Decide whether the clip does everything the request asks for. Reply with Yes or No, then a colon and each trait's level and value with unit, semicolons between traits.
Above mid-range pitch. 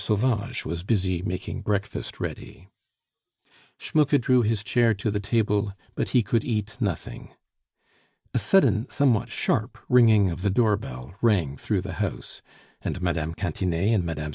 No: low, 105 Hz